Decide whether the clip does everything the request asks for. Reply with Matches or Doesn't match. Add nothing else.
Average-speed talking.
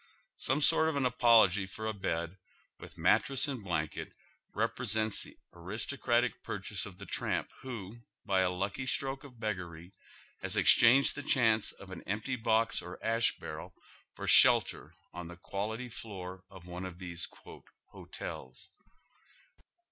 Matches